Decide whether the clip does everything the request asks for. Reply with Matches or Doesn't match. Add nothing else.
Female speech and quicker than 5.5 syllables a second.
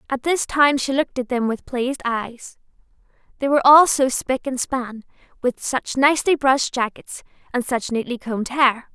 Doesn't match